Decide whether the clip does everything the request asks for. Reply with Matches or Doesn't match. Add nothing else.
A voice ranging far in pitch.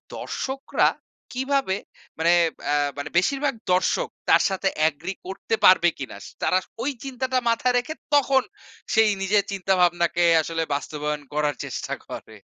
Matches